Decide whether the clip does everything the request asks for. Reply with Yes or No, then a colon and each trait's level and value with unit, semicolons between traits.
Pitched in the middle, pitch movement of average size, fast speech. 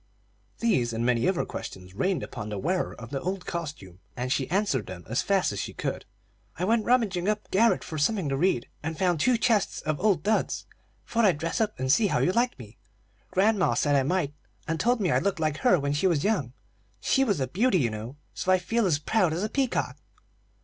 No: medium, 175 Hz; wide, 7.3 semitones; fast, 225 wpm